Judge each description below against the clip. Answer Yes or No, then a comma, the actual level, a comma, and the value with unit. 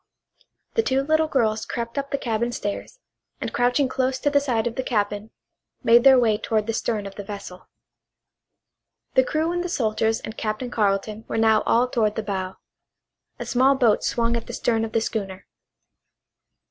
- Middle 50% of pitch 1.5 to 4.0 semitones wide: Yes, average, 3.4 semitones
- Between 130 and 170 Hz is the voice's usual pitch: No, high, 230 Hz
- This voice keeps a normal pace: Yes, average, 185 wpm